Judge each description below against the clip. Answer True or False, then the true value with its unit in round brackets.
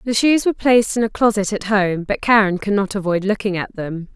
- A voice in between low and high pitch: False (205 Hz)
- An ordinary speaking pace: False (245 wpm)